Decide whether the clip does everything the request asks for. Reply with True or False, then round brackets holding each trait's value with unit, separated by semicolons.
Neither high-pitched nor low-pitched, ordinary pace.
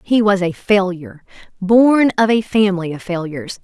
False (195 Hz; 165 wpm)